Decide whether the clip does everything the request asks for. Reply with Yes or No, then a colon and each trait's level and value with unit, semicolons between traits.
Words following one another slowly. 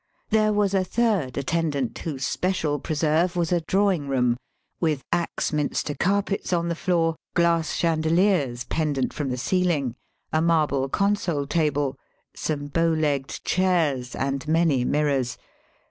Yes: slow, 130 wpm